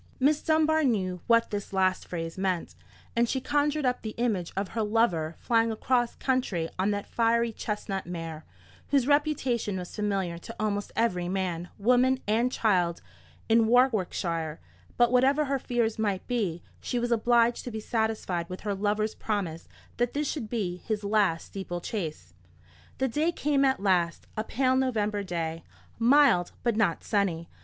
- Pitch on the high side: Yes, high, 215 Hz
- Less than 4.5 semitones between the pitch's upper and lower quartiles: No, average, 5.0 semitones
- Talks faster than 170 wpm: No, average, 165 wpm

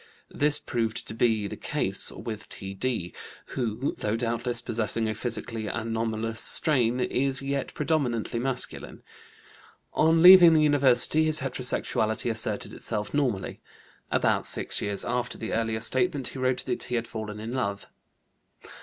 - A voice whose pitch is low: Yes, low, 120 Hz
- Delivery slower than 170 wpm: Yes, average, 140 wpm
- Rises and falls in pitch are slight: No, average, 3.2 semitones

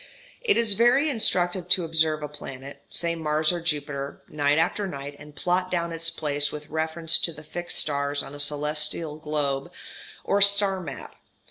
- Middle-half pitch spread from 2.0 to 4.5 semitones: Yes, average, 3.2 semitones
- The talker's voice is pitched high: No, medium, 160 Hz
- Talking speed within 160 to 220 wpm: Yes, average, 170 wpm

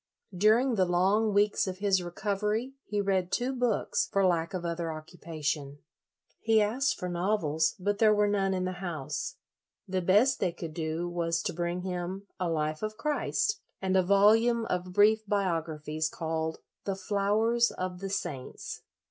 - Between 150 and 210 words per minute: Yes, average, 170 wpm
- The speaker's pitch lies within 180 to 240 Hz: Yes, medium, 185 Hz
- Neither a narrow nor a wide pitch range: Yes, average, 3.6 semitones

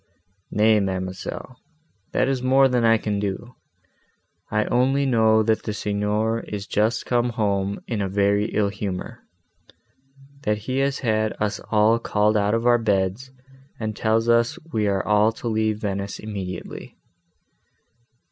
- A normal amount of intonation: No, narrow, 2.3 semitones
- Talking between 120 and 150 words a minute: Yes, average, 145 wpm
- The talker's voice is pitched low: Yes, low, 110 Hz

